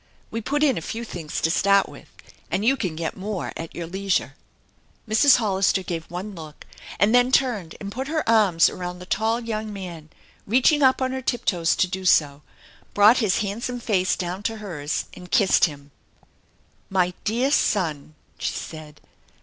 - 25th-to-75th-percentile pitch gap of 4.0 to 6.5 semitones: Yes, average, 4.8 semitones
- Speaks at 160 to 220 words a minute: Yes, average, 185 wpm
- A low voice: No, high, 195 Hz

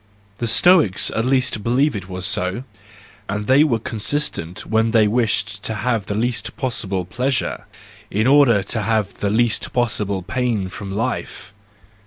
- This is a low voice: Yes, low, 110 Hz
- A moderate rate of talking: Yes, average, 155 wpm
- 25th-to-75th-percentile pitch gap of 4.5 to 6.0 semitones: No, average, 3.6 semitones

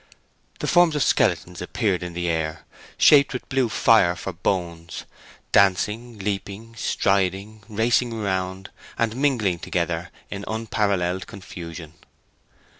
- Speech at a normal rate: No, slow, 115 wpm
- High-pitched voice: No, low, 100 Hz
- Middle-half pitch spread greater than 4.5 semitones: No, average, 4.2 semitones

